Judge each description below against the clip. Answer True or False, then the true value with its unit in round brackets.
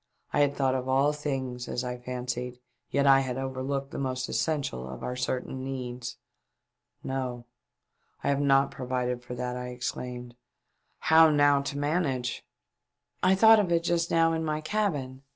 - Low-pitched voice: True (130 Hz)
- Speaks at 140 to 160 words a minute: False (175 wpm)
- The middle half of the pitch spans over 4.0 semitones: False (2.7 semitones)